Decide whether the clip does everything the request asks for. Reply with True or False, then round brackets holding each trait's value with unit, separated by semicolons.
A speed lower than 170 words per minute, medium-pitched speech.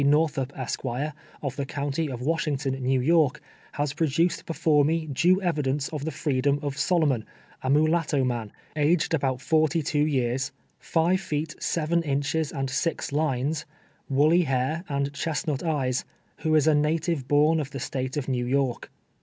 True (160 wpm; 145 Hz)